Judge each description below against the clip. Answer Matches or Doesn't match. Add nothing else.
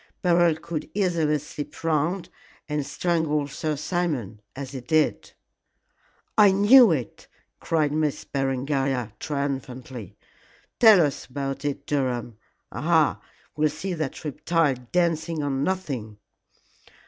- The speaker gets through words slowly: Matches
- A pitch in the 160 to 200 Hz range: Doesn't match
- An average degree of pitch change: Matches